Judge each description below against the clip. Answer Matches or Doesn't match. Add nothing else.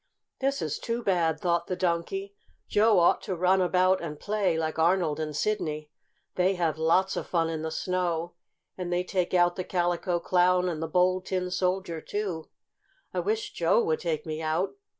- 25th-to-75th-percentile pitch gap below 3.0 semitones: Matches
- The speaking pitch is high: Doesn't match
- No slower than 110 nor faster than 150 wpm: Doesn't match